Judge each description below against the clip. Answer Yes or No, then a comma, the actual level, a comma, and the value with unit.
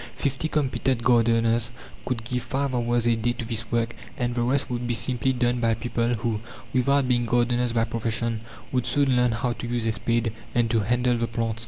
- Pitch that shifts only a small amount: Yes, narrow, 1.3 semitones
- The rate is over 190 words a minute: Yes, fast, 205 wpm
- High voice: No, low, 120 Hz